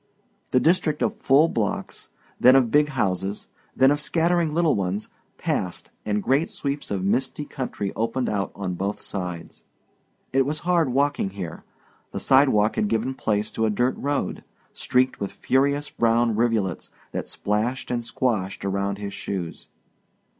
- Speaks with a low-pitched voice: Yes, low, 120 Hz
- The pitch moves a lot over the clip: Yes, wide, 5.7 semitones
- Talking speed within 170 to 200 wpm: No, average, 155 wpm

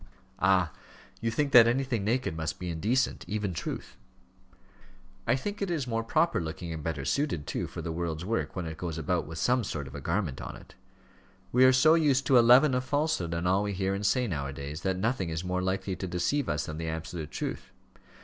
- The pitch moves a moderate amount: No, wide, 7.6 semitones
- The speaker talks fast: Yes, fast, 225 wpm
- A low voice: Yes, very low, 95 Hz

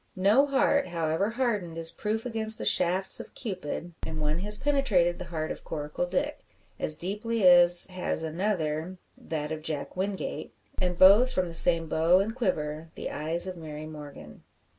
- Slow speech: No, average, 170 wpm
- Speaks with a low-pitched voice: No, medium, 175 Hz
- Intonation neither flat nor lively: Yes, average, 4.6 semitones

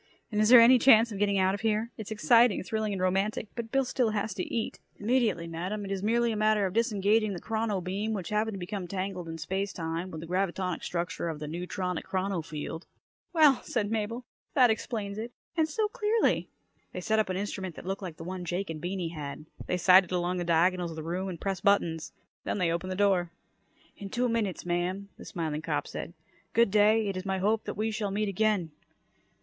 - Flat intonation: No, average, 3.5 semitones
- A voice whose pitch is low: No, high, 195 Hz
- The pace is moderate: No, fast, 220 wpm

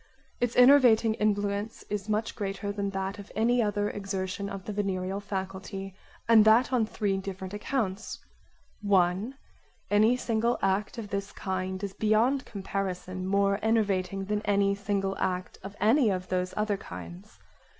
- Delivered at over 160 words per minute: No, average, 150 wpm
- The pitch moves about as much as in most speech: No, narrow, 2.1 semitones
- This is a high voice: Yes, high, 200 Hz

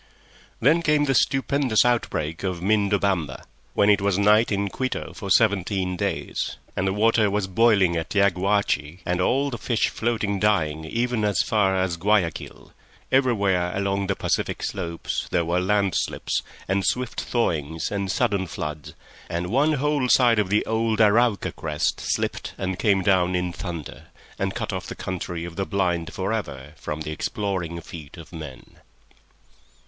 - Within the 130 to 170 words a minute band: Yes, average, 160 wpm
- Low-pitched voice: Yes, low, 100 Hz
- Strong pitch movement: No, average, 3.9 semitones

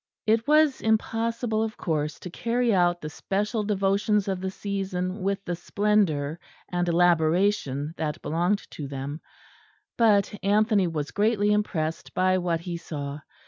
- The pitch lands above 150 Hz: Yes, high, 190 Hz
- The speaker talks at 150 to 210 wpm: No, average, 140 wpm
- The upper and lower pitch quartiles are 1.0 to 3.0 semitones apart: No, average, 4.2 semitones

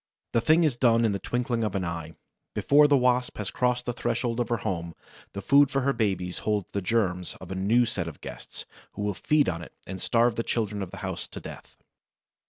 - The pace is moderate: No, fast, 230 wpm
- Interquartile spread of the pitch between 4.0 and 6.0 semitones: Yes, average, 4.6 semitones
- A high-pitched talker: No, low, 115 Hz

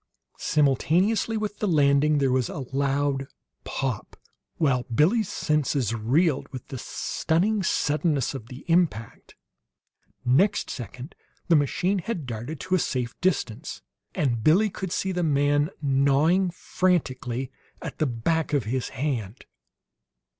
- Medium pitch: Yes, medium, 145 Hz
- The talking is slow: Yes, slow, 130 wpm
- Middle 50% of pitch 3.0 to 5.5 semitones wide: Yes, average, 5.0 semitones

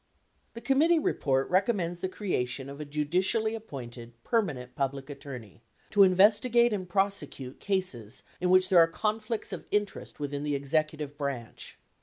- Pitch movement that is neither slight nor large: No, wide, 6.8 semitones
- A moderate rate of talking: Yes, average, 145 wpm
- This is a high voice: No, medium, 165 Hz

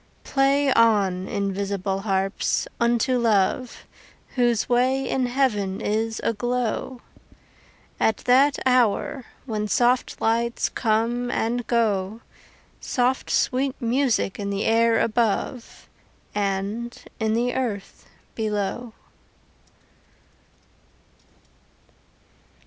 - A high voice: Yes, high, 230 Hz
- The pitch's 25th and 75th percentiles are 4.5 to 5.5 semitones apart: No, average, 3.2 semitones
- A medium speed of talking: No, slow, 85 wpm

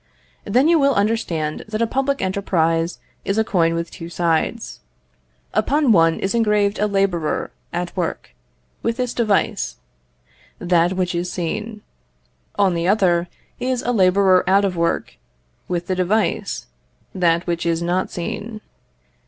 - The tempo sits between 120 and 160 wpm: Yes, average, 145 wpm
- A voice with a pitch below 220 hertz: Yes, high, 190 Hz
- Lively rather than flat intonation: No, average, 4.0 semitones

